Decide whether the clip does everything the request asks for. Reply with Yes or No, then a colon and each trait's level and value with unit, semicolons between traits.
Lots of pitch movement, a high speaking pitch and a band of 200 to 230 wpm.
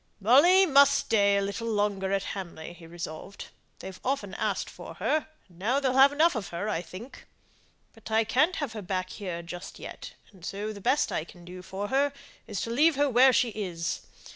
Yes: wide, 6.1 semitones; high, 205 Hz; fast, 205 wpm